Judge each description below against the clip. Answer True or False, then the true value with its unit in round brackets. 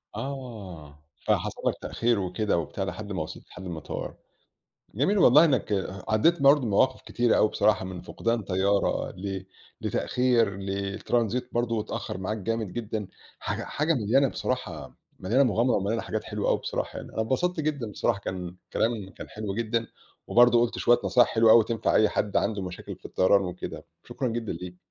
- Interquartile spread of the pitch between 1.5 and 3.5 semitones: False (3.9 semitones)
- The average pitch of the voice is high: False (110 Hz)